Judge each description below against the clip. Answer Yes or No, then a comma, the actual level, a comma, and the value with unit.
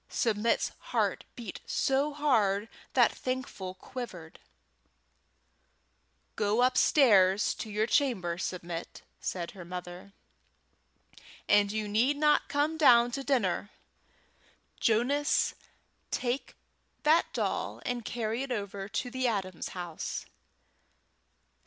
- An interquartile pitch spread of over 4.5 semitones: Yes, average, 5.1 semitones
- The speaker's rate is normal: No, slow, 100 wpm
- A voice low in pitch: No, high, 225 Hz